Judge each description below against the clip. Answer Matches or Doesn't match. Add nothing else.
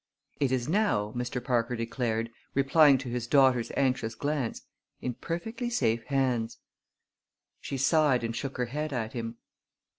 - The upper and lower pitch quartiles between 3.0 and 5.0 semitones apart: Matches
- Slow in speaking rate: Doesn't match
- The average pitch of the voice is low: Matches